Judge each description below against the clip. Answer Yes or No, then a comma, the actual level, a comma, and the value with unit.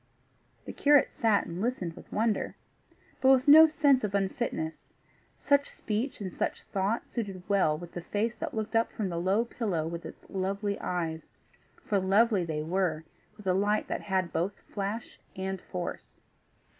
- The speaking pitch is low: No, high, 200 Hz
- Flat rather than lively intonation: No, average, 4.0 semitones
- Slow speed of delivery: No, average, 170 wpm